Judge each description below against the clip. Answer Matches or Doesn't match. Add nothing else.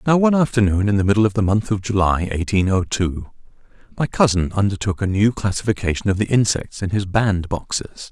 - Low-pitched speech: Matches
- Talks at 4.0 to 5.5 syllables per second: Doesn't match